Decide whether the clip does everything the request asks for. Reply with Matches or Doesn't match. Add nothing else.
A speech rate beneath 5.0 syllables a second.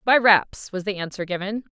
Doesn't match